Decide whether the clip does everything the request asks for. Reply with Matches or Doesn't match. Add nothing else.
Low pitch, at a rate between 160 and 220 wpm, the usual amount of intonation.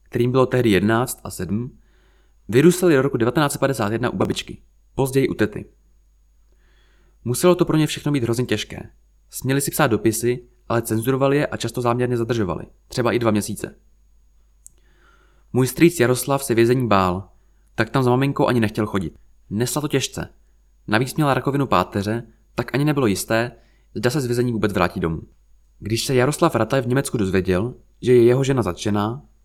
Matches